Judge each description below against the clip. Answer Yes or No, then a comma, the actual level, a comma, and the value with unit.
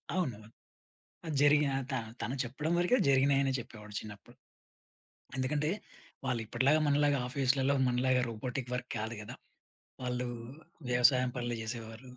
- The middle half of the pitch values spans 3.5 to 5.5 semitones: No, average, 2.7 semitones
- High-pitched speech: No, low, 130 Hz